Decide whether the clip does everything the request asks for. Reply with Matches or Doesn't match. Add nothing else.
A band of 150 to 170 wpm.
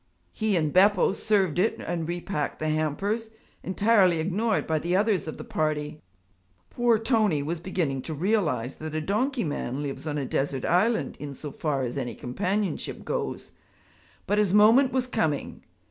Matches